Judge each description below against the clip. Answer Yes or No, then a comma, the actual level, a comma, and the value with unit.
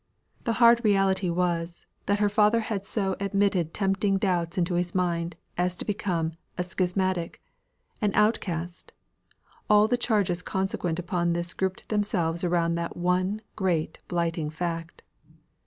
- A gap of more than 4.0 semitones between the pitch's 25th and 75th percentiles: No, average, 2.9 semitones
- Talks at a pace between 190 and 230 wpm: No, average, 140 wpm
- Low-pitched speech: No, medium, 180 Hz